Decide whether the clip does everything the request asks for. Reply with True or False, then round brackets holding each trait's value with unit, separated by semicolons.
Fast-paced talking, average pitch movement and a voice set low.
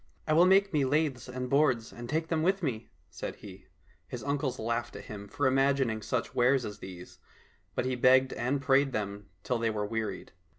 True (215 wpm; 3.9 semitones; 130 Hz)